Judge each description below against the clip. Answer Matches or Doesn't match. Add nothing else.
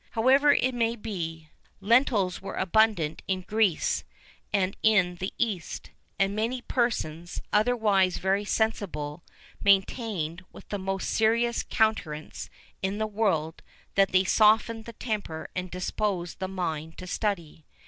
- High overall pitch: Matches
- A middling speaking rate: Doesn't match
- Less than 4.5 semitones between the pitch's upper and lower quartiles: Matches